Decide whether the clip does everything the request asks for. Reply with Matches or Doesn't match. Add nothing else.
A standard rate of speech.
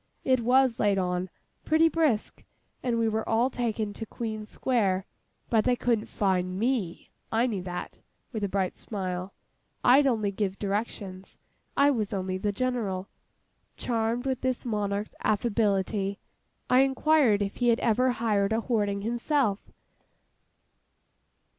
Doesn't match